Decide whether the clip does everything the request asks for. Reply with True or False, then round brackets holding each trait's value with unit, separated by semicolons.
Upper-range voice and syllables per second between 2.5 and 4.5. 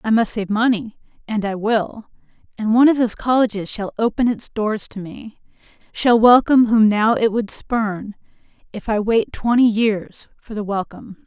False (220 Hz; 4.8 syllables/s)